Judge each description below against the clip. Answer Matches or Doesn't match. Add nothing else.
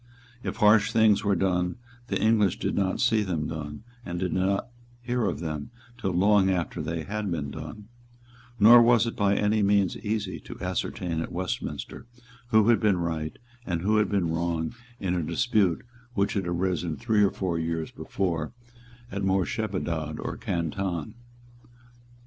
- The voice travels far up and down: Doesn't match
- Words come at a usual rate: Matches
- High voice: Doesn't match